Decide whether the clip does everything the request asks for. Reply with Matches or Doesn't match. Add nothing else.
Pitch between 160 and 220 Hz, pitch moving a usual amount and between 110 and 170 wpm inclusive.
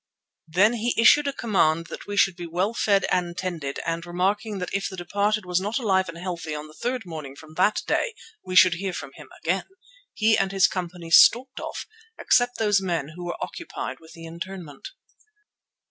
Doesn't match